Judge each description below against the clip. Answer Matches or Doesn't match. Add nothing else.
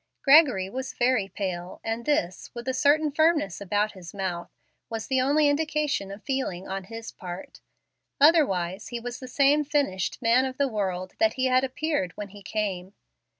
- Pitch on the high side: Matches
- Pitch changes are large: Matches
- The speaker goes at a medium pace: Matches